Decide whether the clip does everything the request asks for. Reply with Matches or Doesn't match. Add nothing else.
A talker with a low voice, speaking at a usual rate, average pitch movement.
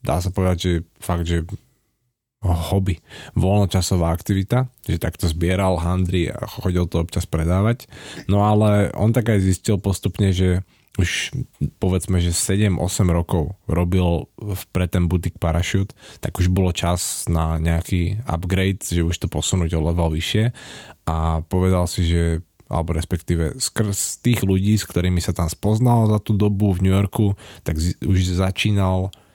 Matches